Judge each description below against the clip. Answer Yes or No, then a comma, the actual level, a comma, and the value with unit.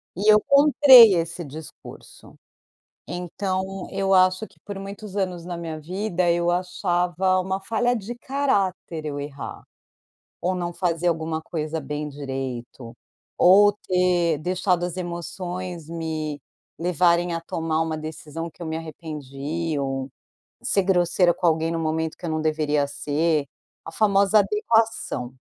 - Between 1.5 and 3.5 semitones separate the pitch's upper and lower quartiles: Yes, average, 3.1 semitones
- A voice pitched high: No, medium, 175 Hz